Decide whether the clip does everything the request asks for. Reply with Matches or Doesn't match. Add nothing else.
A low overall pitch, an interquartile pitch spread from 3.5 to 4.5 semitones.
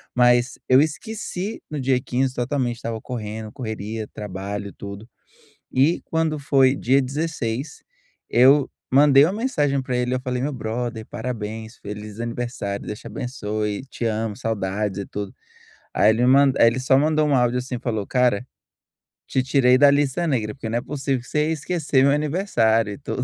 Matches